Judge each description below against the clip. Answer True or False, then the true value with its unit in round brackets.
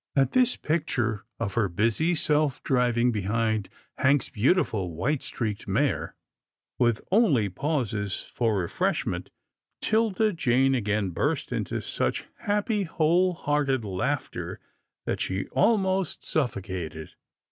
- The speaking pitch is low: True (125 Hz)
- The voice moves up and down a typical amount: False (7.4 semitones)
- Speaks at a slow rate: True (115 wpm)